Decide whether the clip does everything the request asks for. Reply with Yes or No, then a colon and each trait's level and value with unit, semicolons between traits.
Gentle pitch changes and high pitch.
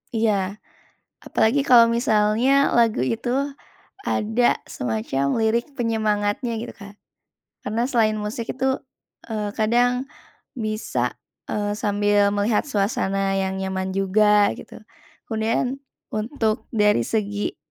Yes: narrow, 2.0 semitones; high, 215 Hz